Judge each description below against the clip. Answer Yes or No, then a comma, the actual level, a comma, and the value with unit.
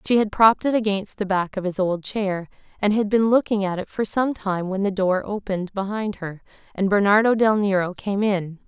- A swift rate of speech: Yes, fast, 220 wpm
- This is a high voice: Yes, high, 200 Hz